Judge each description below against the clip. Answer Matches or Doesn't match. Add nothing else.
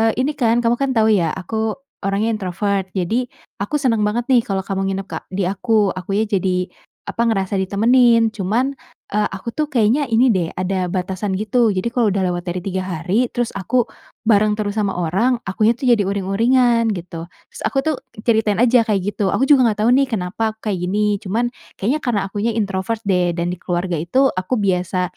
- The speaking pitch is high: Matches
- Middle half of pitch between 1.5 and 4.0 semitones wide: Matches